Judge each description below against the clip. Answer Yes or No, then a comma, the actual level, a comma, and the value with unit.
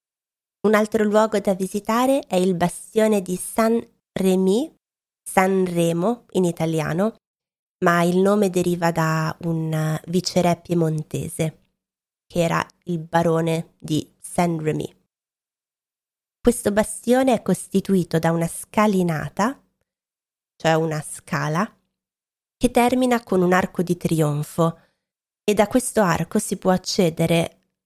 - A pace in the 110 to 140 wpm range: Yes, average, 120 wpm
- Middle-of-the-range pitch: Yes, medium, 180 Hz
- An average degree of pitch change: Yes, average, 4.2 semitones